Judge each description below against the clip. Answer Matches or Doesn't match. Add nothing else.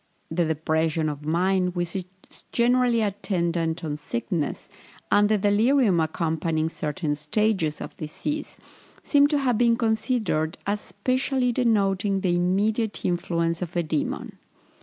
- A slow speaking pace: Matches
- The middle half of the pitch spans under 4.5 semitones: Doesn't match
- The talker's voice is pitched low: Doesn't match